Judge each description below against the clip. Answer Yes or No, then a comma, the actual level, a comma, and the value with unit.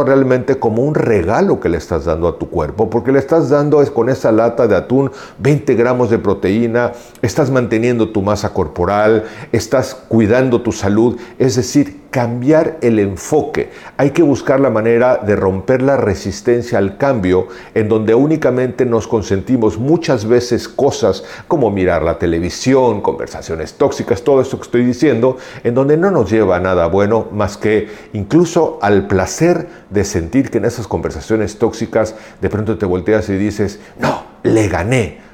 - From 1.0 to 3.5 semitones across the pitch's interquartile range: No, average, 4.0 semitones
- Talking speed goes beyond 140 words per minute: Yes, average, 165 wpm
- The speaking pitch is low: Yes, low, 115 Hz